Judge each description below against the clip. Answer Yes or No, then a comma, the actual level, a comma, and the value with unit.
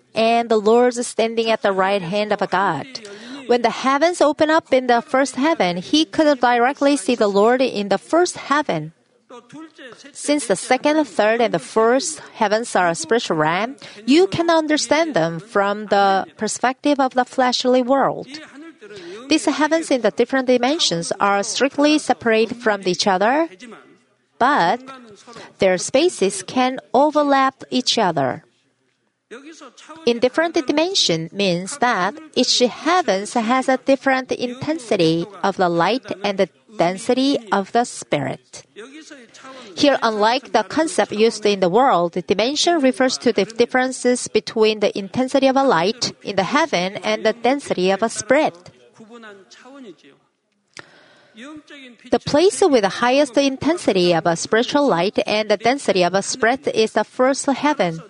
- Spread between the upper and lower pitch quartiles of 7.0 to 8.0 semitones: No, wide, 5.4 semitones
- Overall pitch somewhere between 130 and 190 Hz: No, high, 245 Hz